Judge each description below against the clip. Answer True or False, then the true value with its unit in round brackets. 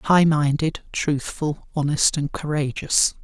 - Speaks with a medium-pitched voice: True (150 Hz)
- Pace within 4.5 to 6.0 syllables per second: False (3.7 syllables/s)